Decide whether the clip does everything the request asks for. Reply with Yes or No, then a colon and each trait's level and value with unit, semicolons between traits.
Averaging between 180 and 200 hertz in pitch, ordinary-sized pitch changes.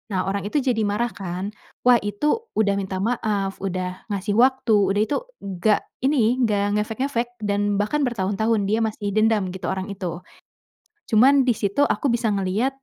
No: high, 210 Hz; average, 3.4 semitones